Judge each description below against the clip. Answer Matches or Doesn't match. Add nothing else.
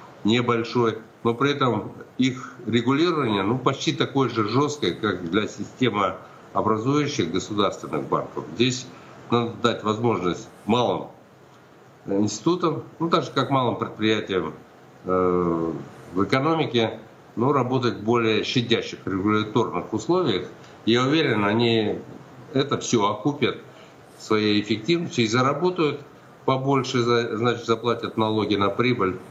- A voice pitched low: Matches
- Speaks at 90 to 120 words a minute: Matches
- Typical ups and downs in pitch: Matches